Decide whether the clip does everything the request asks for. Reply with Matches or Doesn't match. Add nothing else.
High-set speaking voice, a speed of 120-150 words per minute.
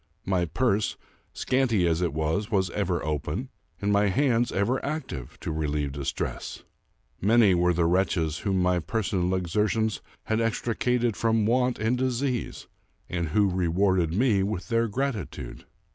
Doesn't match